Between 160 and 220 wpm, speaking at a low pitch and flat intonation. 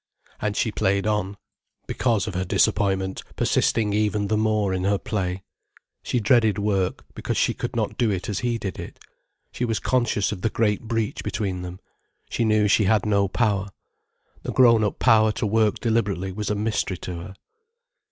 Yes: average, 180 wpm; low, 105 Hz; narrow, 2.2 semitones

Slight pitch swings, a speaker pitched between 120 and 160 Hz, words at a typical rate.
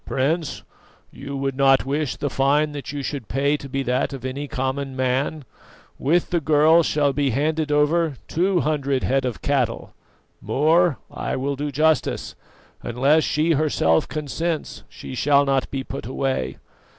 Yes: narrow, 2.3 semitones; medium, 140 Hz; average, 160 wpm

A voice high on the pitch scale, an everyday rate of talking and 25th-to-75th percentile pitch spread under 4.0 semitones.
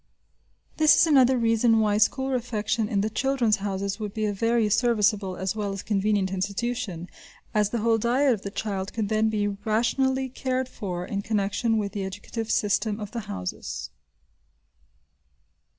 Yes: high, 215 Hz; average, 165 wpm; average, 2.8 semitones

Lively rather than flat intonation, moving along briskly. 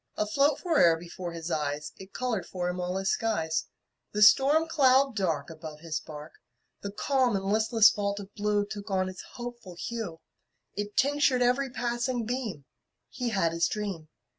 No: wide, 5.9 semitones; average, 165 wpm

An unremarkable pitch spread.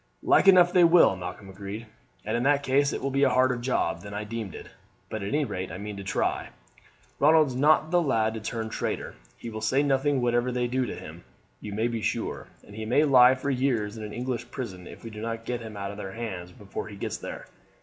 Yes: average, 4.3 semitones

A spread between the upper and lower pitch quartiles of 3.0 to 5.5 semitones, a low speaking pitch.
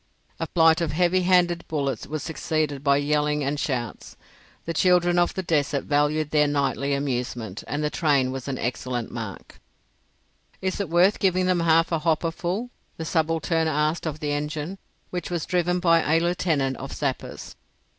No: average, 3.4 semitones; medium, 155 Hz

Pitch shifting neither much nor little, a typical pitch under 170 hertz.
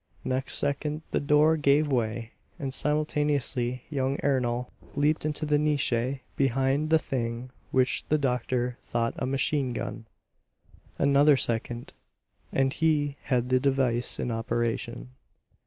Yes: average, 3.2 semitones; low, 135 Hz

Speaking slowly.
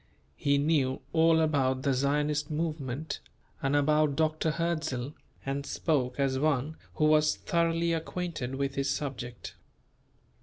Yes: slow, 125 wpm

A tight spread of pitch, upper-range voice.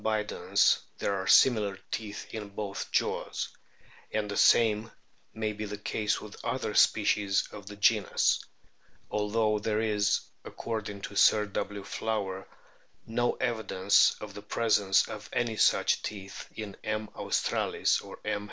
No: narrow, 1.3 semitones; low, 105 Hz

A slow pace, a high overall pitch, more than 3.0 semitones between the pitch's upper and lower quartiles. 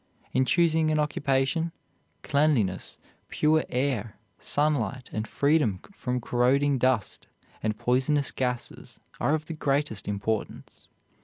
No: slow, 110 wpm; low, 135 Hz; average, 3.8 semitones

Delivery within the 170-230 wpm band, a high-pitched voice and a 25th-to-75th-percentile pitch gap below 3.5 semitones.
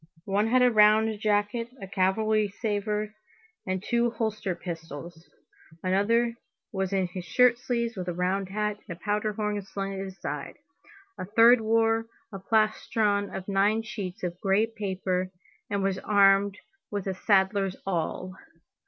No: average, 155 wpm; high, 205 Hz; narrow, 2.4 semitones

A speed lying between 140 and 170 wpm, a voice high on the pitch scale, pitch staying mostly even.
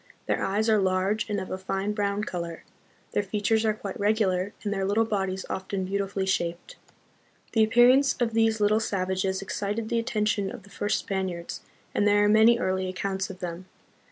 No: average, 190 wpm; high, 200 Hz; narrow, 2.3 semitones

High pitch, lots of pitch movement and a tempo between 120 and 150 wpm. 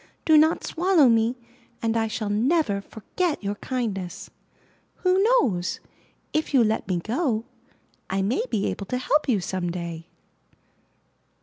Yes: high, 225 Hz; wide, 7.5 semitones; slow, 135 wpm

